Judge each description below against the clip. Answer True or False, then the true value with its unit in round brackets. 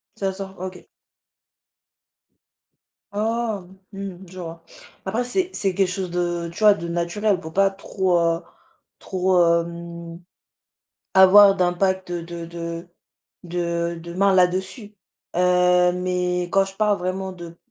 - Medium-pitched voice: True (180 Hz)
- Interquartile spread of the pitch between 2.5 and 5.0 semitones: False (2.1 semitones)